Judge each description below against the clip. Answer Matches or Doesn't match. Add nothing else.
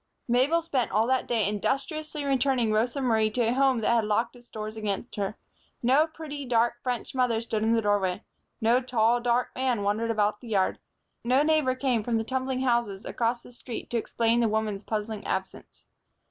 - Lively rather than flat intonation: Doesn't match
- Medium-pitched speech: Doesn't match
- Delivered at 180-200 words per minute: Matches